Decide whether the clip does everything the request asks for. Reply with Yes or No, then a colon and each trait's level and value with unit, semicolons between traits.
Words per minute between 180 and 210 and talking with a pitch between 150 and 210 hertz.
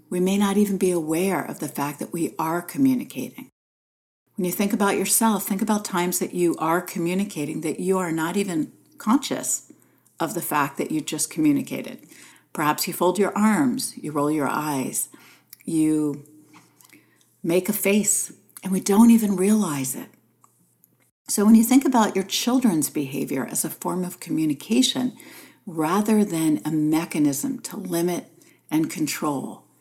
No: average, 155 wpm; medium, 185 Hz